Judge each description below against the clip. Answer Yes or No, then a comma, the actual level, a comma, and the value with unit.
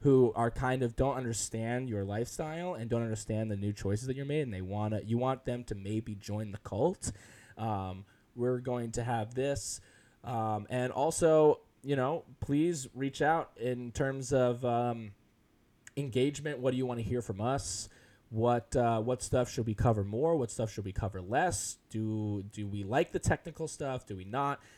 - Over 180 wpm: Yes, average, 190 wpm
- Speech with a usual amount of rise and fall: Yes, average, 3.4 semitones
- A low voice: Yes, low, 120 Hz